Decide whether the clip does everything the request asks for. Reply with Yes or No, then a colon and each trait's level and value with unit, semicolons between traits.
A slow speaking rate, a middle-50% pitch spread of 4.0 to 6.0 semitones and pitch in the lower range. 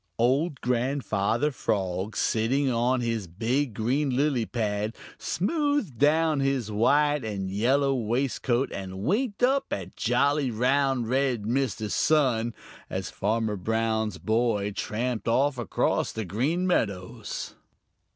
Yes: slow, 120 wpm; average, 4.3 semitones; low, 120 Hz